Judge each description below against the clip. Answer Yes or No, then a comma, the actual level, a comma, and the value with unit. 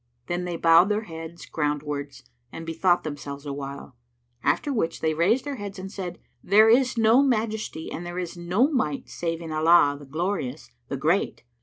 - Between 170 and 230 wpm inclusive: Yes, average, 175 wpm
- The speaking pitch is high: No, medium, 170 Hz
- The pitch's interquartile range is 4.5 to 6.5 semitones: Yes, average, 5.2 semitones